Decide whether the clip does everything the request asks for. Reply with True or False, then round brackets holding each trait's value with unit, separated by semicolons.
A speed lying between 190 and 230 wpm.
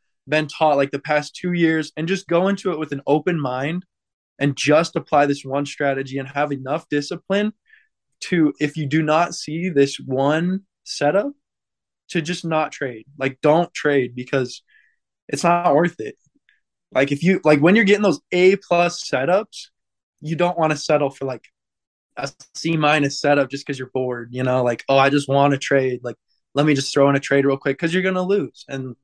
True (205 wpm)